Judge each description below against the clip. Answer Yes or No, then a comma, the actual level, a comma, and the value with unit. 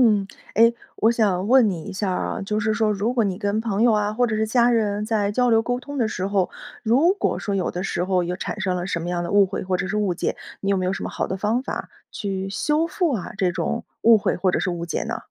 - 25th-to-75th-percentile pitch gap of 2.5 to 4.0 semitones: Yes, average, 3.4 semitones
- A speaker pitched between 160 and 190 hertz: No, high, 205 Hz